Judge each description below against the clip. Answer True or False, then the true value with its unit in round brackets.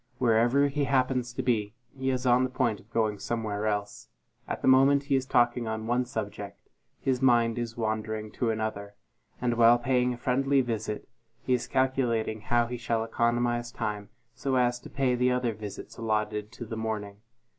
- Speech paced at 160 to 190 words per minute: True (185 wpm)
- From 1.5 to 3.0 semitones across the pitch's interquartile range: True (2.5 semitones)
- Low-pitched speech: True (120 Hz)